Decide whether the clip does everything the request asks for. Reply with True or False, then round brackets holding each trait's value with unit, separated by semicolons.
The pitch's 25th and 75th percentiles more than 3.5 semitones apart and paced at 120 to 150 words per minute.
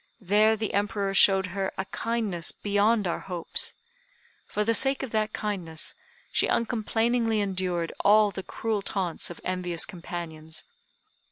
False (3.1 semitones; 140 wpm)